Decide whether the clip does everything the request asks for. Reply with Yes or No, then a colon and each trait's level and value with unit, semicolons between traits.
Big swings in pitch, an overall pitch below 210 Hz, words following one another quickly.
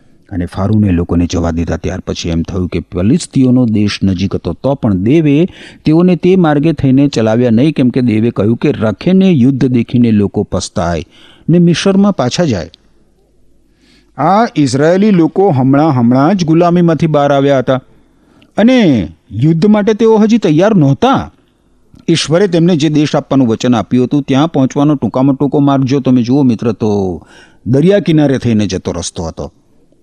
Yes: wide, 7.6 semitones; low, 135 Hz; fast, 155 wpm